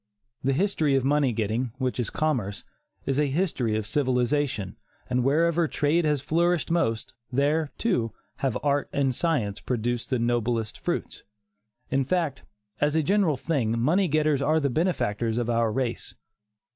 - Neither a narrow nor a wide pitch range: Yes, average, 4.5 semitones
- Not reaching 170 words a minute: Yes, average, 155 wpm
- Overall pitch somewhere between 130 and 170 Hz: Yes, low, 135 Hz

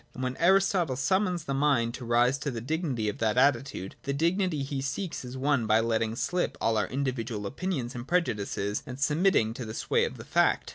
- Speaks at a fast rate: Yes, fast, 210 wpm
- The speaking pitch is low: Yes, low, 130 Hz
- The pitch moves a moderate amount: Yes, average, 5.0 semitones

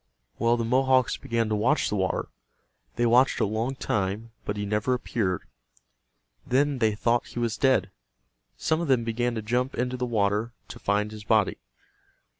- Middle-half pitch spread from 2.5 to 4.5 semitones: Yes, average, 3.0 semitones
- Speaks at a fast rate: No, average, 175 wpm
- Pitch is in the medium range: No, low, 115 Hz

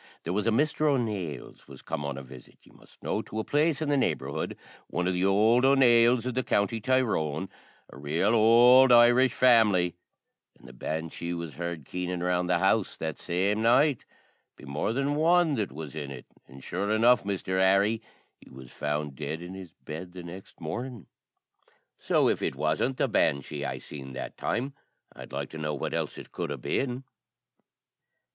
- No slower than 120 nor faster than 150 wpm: No, average, 185 wpm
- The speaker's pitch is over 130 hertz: No, very low, 95 Hz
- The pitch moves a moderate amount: No, wide, 7.5 semitones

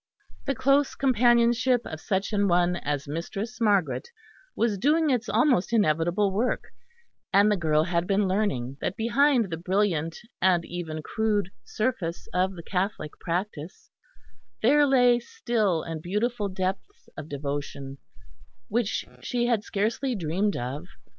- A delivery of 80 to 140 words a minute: Yes, slow, 135 wpm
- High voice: Yes, high, 200 Hz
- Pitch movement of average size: No, wide, 5.8 semitones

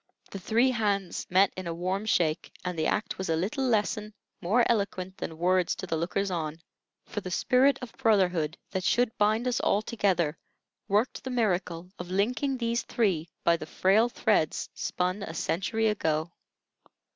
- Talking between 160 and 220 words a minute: Yes, average, 170 wpm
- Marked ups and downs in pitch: No, average, 4.2 semitones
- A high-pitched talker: Yes, high, 195 Hz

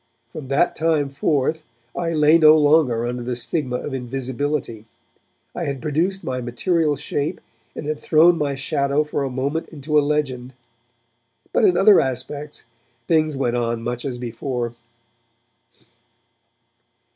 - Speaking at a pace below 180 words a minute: Yes, average, 140 wpm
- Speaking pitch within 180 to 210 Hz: No, medium, 140 Hz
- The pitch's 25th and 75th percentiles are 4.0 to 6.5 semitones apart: No, average, 3.6 semitones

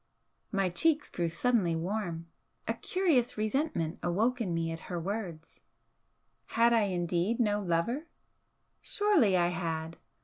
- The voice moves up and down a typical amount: No, wide, 5.8 semitones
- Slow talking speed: Yes, slow, 130 wpm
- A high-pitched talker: Yes, high, 195 Hz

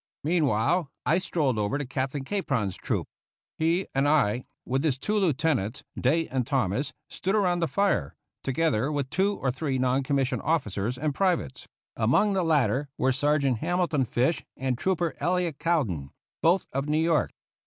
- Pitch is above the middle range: No, medium, 145 Hz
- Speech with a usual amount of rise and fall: Yes, average, 4.5 semitones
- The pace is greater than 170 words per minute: No, average, 160 wpm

